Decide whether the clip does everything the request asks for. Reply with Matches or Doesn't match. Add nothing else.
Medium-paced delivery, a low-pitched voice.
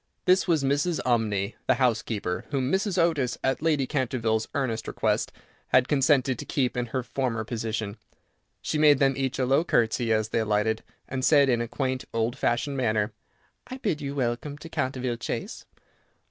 Matches